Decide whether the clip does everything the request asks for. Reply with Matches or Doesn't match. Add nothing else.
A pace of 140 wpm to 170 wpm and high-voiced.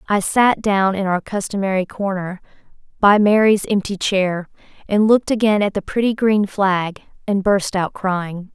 Matches